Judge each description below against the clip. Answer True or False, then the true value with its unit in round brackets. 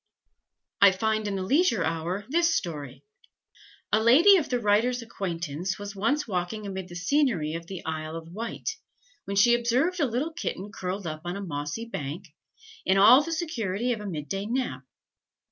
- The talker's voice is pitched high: True (200 Hz)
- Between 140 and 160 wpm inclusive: False (180 wpm)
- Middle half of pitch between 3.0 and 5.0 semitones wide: False (5.6 semitones)